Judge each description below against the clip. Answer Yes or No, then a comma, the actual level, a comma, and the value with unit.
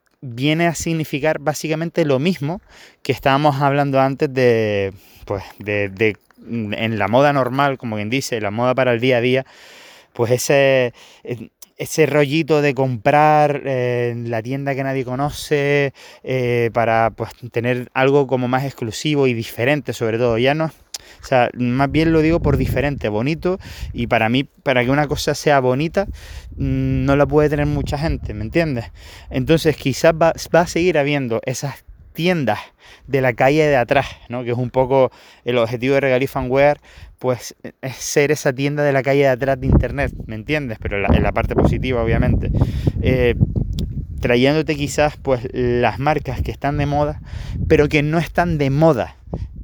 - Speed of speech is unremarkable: Yes, average, 170 wpm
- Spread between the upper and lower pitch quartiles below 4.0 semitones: Yes, average, 3.6 semitones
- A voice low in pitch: Yes, low, 130 Hz